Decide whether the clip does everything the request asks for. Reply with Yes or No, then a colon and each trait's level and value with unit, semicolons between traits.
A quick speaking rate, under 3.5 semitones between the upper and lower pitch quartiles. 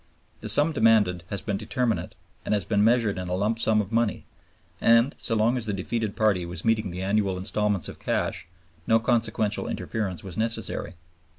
No: average, 185 wpm; narrow, 2.6 semitones